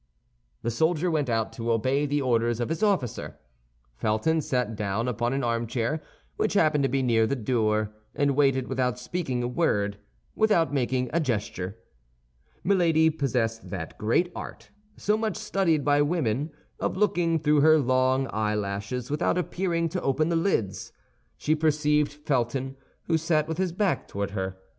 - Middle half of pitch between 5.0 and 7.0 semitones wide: Yes, wide, 5.6 semitones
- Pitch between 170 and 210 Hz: No, low, 135 Hz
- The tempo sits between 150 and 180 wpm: Yes, average, 160 wpm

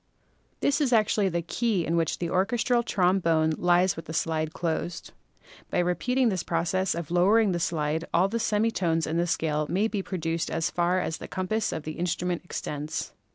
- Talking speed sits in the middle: Yes, average, 190 wpm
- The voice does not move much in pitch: No, average, 3.1 semitones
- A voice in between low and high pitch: Yes, medium, 175 Hz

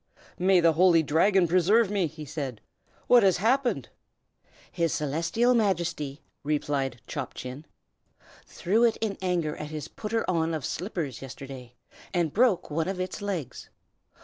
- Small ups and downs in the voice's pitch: No, average, 4.8 semitones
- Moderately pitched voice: Yes, medium, 170 Hz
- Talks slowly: No, average, 145 wpm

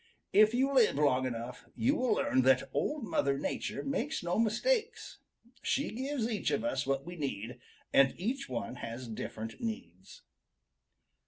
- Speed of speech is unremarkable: Yes, average, 155 wpm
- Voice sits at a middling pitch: Yes, medium, 180 Hz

